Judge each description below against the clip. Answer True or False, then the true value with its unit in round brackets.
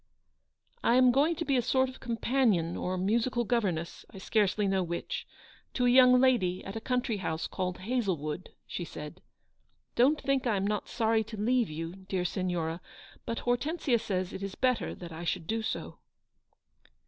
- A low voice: False (215 Hz)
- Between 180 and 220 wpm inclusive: True (185 wpm)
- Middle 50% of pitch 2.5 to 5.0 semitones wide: False (5.4 semitones)